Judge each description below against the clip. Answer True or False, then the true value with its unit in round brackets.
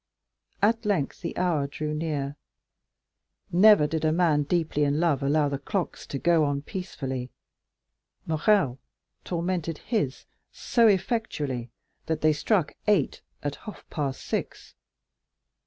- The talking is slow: True (125 wpm)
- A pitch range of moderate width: True (4.3 semitones)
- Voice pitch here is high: False (155 Hz)